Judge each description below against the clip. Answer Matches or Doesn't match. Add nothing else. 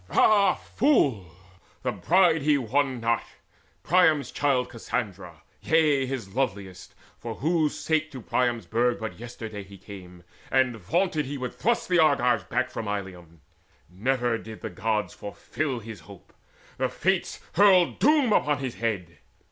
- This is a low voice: Matches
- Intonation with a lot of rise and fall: Matches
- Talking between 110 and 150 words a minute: Matches